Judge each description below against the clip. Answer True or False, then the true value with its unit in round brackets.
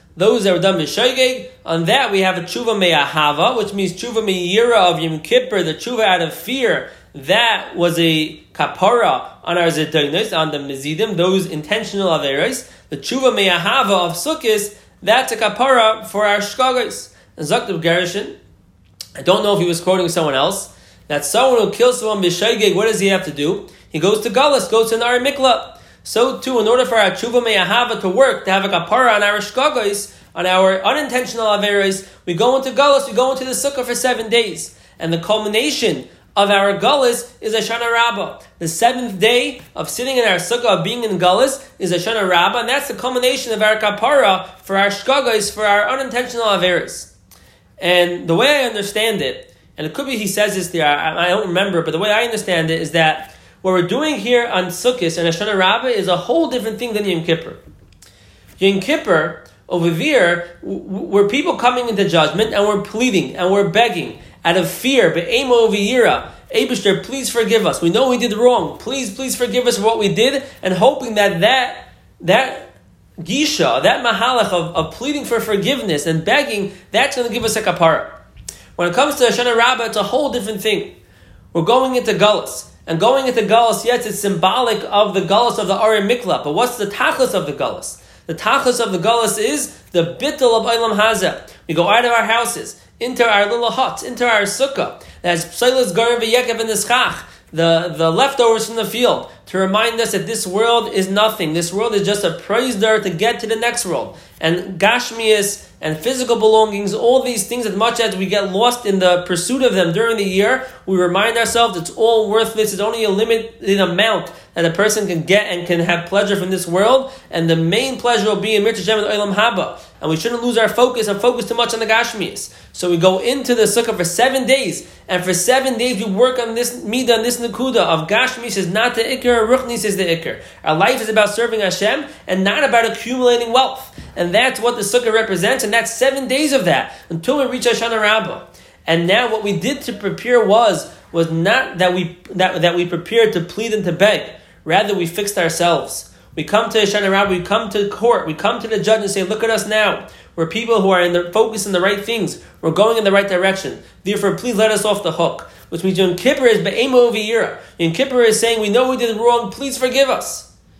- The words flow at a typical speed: False (210 wpm)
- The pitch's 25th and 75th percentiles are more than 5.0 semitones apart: False (4.5 semitones)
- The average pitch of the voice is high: True (215 Hz)